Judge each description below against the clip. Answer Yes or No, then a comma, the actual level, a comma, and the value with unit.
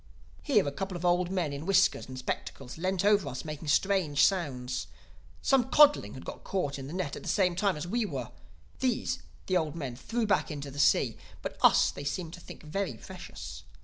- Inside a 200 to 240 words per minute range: Yes, fast, 205 wpm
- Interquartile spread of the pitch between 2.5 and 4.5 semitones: No, wide, 5.5 semitones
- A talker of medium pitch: Yes, medium, 175 Hz